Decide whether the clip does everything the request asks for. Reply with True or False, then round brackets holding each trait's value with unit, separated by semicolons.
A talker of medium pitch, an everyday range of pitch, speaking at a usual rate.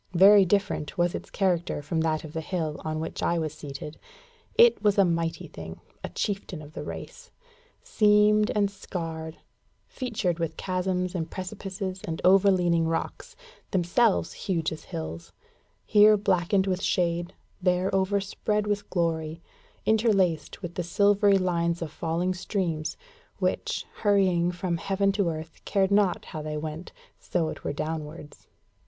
True (180 Hz; 3.4 semitones; 150 wpm)